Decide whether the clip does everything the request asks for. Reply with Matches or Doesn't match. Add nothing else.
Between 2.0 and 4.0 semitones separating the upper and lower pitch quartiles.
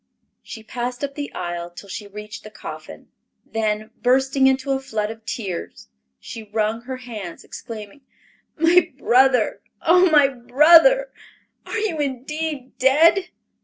Doesn't match